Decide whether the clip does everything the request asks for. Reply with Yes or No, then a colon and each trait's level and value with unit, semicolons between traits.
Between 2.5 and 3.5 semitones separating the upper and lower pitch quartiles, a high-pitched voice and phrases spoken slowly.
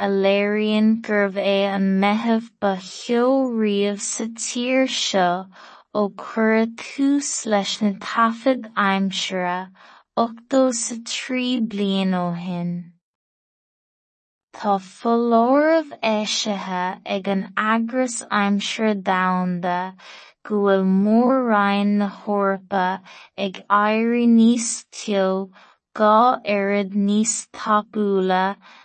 Yes: average, 2.8 semitones; high, 205 Hz; slow, 60 wpm